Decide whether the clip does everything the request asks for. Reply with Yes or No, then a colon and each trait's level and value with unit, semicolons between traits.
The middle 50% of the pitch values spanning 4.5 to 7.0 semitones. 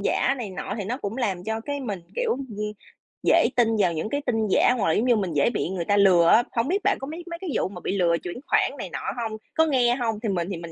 Yes: average, 5.1 semitones